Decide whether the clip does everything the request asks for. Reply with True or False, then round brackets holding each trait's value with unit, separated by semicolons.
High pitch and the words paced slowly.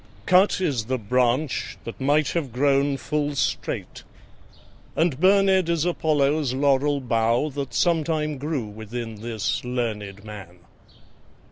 False (140 Hz; 120 wpm)